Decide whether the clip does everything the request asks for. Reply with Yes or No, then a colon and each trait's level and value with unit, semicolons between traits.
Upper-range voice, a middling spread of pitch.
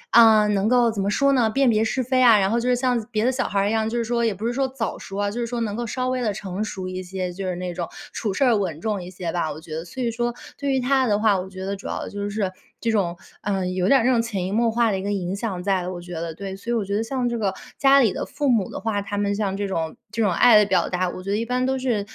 Yes: high, 210 Hz; average, 3.8 semitones